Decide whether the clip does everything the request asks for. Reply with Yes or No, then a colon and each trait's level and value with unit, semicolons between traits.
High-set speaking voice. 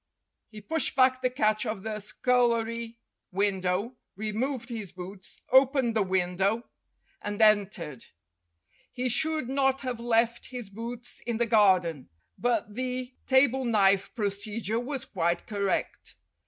Yes: high, 225 Hz